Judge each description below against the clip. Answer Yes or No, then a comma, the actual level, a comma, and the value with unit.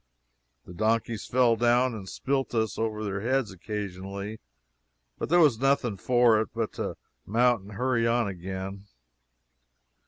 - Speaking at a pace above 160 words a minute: No, average, 145 wpm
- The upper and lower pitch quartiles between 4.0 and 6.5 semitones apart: No, average, 3.5 semitones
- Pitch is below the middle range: Yes, low, 110 Hz